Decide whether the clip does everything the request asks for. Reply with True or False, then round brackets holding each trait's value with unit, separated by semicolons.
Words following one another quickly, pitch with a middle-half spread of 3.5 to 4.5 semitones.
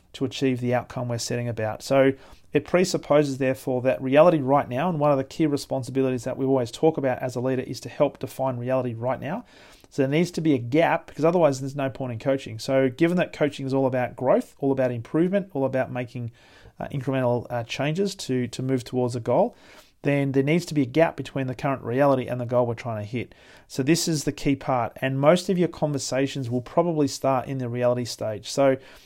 False (230 wpm; 2.5 semitones)